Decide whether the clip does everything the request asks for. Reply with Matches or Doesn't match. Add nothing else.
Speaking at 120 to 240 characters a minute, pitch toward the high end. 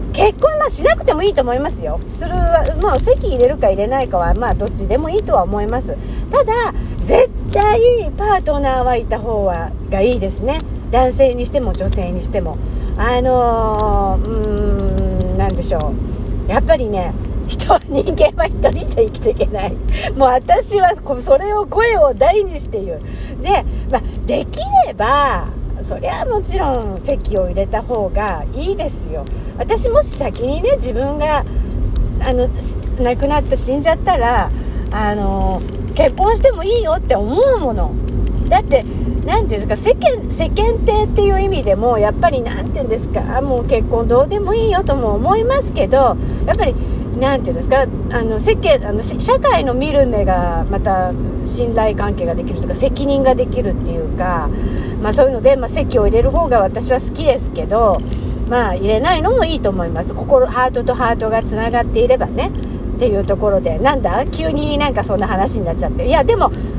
Doesn't match